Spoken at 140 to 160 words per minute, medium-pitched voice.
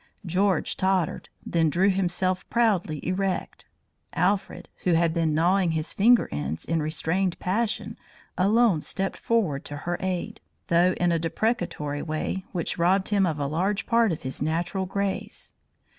Yes: average, 150 wpm; medium, 180 Hz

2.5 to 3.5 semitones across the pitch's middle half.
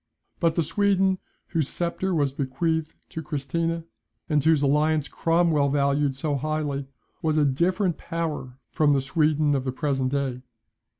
Yes: average, 3.0 semitones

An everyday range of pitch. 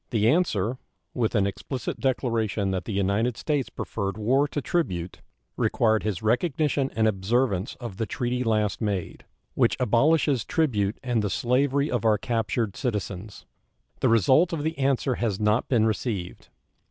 Yes: average, 4.1 semitones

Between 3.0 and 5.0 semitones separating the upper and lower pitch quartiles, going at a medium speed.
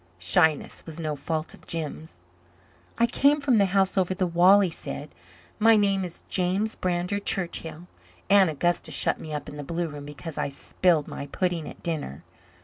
Yes: average, 3.9 semitones; average, 180 wpm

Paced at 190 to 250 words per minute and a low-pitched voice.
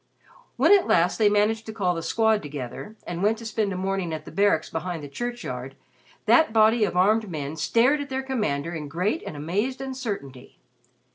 No: average, 195 wpm; high, 200 Hz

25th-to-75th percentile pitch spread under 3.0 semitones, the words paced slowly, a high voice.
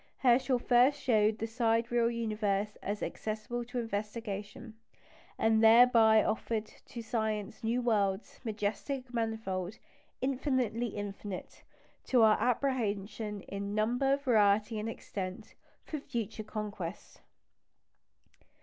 Yes: narrow, 2.5 semitones; slow, 105 wpm; high, 220 Hz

